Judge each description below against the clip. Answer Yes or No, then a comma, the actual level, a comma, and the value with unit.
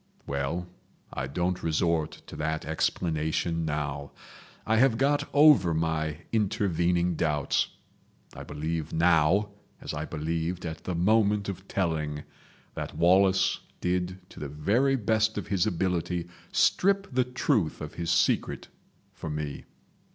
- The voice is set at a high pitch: No, very low, 85 Hz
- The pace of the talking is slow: Yes, slow, 130 wpm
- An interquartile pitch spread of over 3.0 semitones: Yes, average, 4.1 semitones